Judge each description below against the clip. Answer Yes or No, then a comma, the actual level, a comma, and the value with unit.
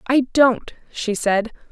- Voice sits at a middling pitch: No, high, 235 Hz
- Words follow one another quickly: No, average, 140 wpm